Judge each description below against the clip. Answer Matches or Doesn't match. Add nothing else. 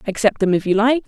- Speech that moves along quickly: Matches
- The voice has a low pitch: Doesn't match